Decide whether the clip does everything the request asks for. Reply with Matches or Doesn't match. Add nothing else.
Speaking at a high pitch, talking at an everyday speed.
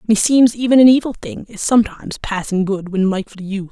Matches